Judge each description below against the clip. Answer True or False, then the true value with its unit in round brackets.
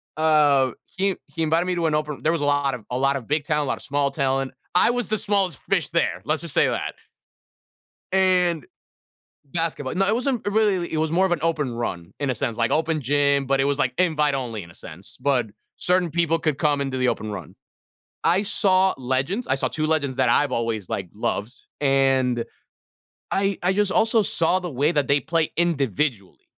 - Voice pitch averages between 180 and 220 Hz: False (150 Hz)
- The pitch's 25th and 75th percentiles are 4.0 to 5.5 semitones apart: True (4.6 semitones)